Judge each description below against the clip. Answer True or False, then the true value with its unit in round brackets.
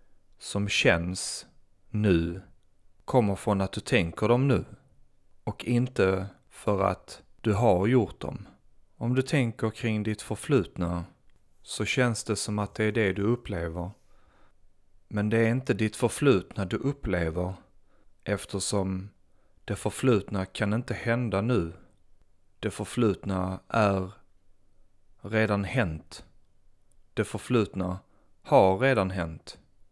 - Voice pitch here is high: False (100 Hz)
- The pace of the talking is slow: True (120 wpm)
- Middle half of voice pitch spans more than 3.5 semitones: False (2.8 semitones)